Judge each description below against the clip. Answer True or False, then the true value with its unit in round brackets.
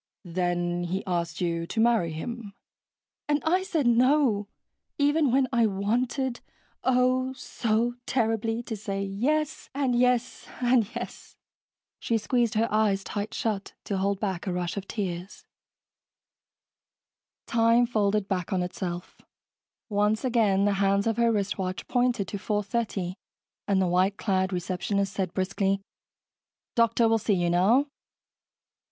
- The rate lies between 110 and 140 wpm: True (135 wpm)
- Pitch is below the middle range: False (210 Hz)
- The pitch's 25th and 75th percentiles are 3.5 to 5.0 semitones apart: True (3.9 semitones)